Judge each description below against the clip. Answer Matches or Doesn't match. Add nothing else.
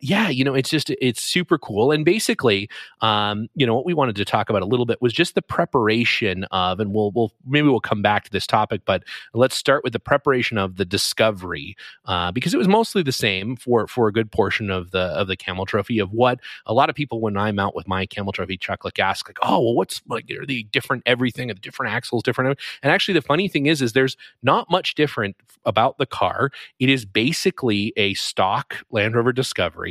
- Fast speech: Matches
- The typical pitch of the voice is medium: Doesn't match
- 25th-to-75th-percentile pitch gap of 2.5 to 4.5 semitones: Doesn't match